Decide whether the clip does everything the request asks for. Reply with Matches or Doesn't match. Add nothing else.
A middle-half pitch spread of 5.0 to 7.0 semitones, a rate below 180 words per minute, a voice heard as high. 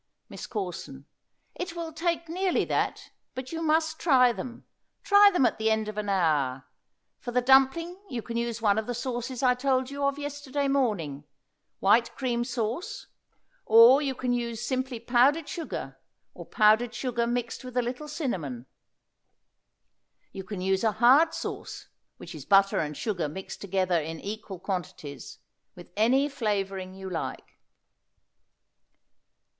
Matches